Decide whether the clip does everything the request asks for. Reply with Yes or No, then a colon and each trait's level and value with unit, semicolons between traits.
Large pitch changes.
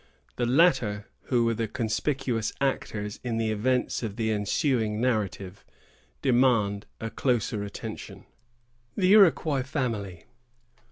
No: average, 3.7 semitones